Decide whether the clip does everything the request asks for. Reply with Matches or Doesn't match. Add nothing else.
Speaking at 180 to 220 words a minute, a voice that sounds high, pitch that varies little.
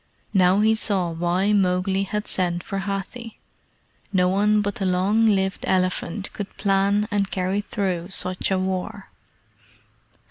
Doesn't match